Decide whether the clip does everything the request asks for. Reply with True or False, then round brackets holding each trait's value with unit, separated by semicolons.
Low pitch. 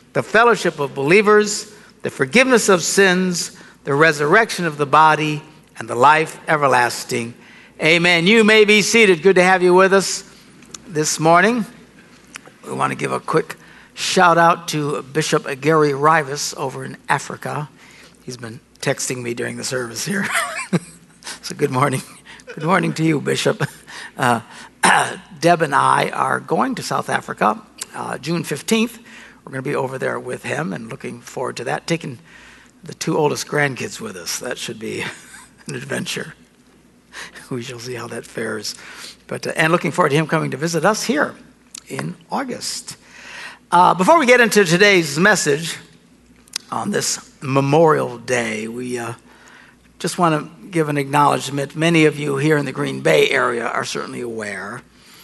False (160 Hz)